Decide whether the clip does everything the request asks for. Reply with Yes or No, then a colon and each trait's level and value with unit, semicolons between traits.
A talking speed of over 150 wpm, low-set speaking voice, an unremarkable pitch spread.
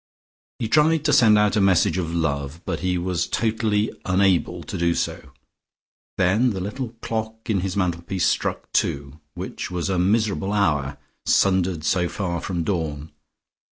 Yes: average, 160 wpm; very low, 95 Hz; average, 3.8 semitones